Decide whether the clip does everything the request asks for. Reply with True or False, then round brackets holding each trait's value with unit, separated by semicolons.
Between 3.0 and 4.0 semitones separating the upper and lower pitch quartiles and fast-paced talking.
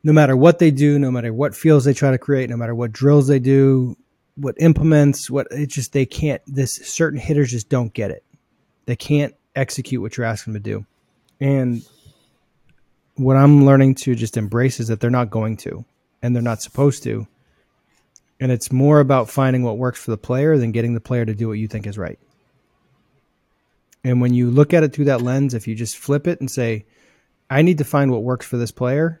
True (3.4 semitones; 220 wpm)